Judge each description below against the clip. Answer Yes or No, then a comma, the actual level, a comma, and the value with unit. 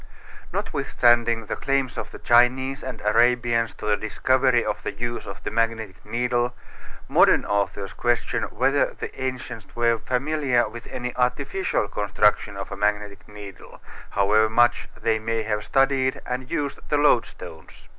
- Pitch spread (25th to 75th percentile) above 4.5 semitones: No, average, 3.3 semitones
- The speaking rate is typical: Yes, average, 145 wpm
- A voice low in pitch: Yes, low, 120 Hz